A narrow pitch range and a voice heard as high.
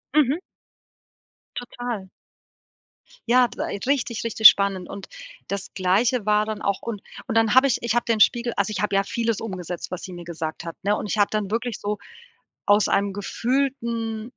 No: average, 3.0 semitones; high, 215 Hz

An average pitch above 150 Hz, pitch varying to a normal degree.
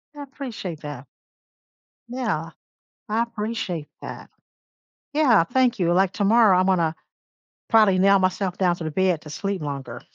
Yes: high, 190 Hz; average, 5.0 semitones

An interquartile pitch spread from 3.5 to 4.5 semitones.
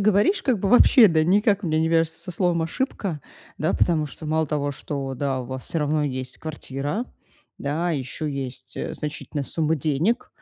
Yes: average, 4.0 semitones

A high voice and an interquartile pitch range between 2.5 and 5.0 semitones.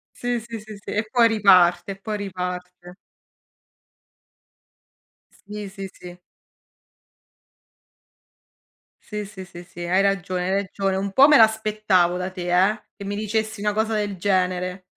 Yes: high, 195 Hz; average, 2.8 semitones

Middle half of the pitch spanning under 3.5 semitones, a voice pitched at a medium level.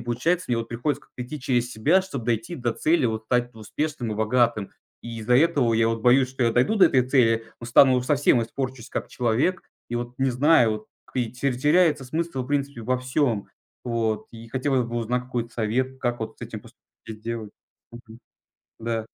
No: average, 2.7 semitones; low, 125 Hz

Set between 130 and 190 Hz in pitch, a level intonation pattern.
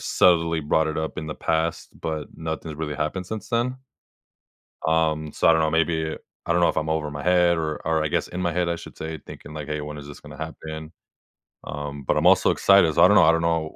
No: very low, 80 Hz; narrow, 1.5 semitones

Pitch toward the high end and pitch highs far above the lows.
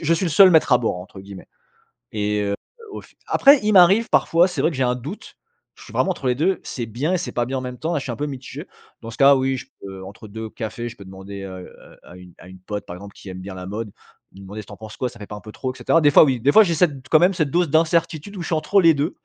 No: low, 130 Hz; wide, 8.0 semitones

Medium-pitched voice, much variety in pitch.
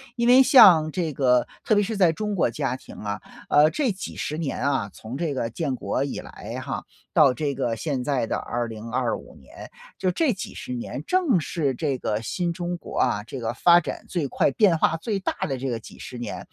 Yes: medium, 145 Hz; wide, 6.0 semitones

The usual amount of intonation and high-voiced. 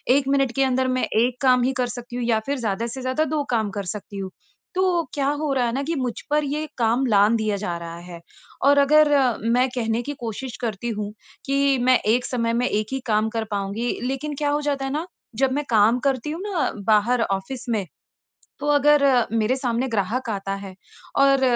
Yes: average, 3.9 semitones; very high, 250 Hz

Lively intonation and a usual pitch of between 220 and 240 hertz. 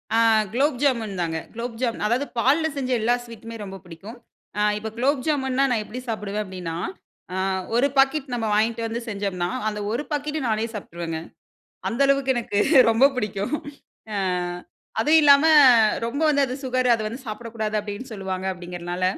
No: average, 4.3 semitones; high, 230 Hz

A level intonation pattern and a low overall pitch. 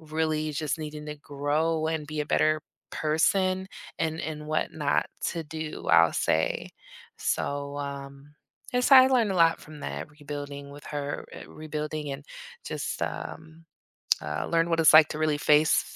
No: narrow, 1.7 semitones; medium, 155 Hz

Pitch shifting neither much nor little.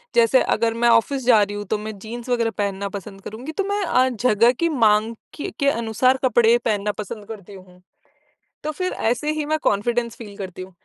Yes: average, 3.6 semitones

